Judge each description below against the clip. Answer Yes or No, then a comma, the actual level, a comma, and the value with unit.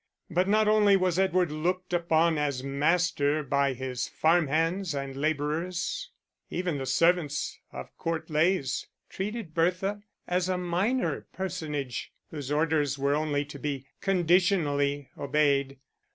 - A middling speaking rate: No, slow, 130 wpm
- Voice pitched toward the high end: No, medium, 160 Hz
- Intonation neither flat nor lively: Yes, average, 4.2 semitones